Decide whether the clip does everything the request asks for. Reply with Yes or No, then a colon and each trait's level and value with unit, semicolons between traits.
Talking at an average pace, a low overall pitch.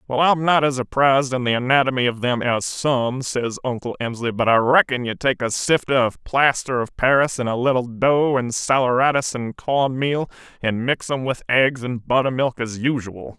Yes: average, 195 wpm; low, 130 Hz